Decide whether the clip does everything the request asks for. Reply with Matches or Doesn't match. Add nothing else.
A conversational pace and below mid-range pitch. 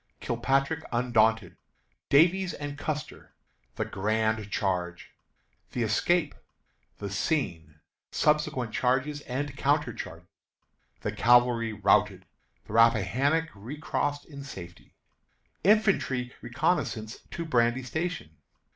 Doesn't match